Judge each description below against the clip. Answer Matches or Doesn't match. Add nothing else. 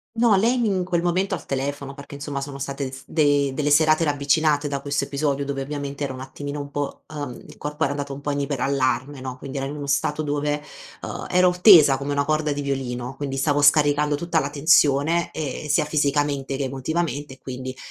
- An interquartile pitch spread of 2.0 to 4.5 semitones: Doesn't match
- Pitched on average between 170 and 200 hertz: Doesn't match